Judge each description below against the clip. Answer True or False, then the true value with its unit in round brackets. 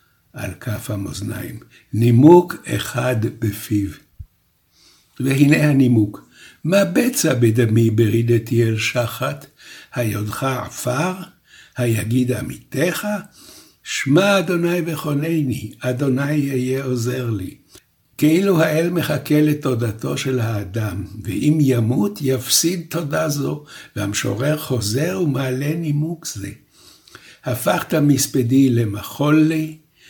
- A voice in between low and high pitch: False (130 Hz)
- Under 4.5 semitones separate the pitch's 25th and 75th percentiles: False (5.1 semitones)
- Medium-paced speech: False (90 wpm)